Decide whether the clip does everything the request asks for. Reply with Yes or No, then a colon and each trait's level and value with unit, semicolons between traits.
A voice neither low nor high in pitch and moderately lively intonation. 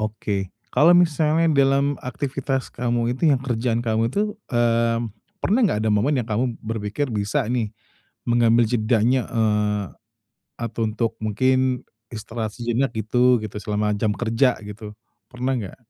No: low, 115 Hz; average, 3.2 semitones